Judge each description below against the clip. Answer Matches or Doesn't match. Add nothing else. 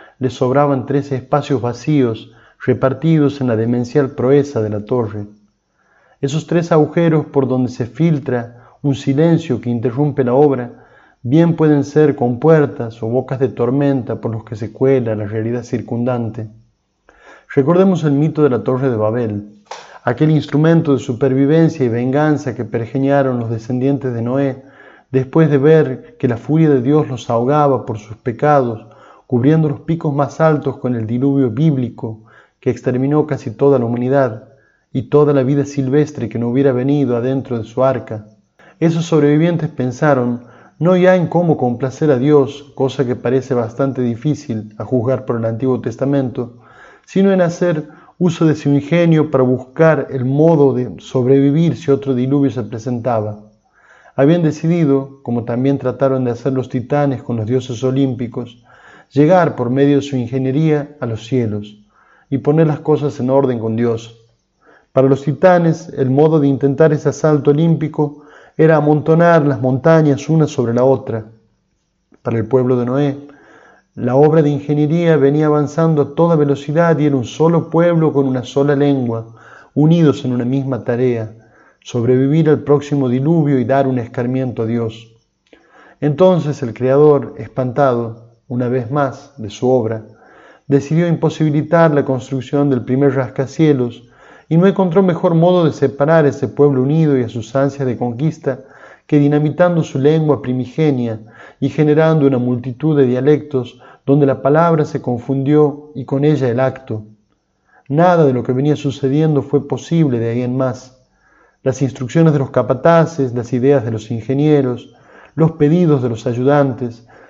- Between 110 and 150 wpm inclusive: Doesn't match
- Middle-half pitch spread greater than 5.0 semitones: Doesn't match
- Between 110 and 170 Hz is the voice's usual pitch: Matches